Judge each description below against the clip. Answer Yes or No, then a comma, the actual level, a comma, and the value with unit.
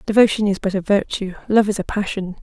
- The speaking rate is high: Yes, fast, 225 wpm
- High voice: Yes, high, 200 Hz